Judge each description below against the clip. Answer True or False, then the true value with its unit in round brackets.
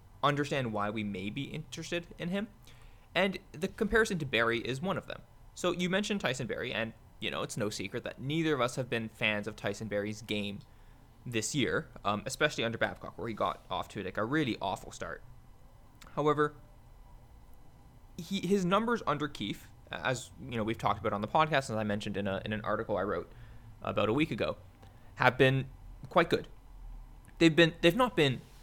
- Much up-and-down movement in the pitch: True (6.0 semitones)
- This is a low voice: True (120 Hz)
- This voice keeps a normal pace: True (195 wpm)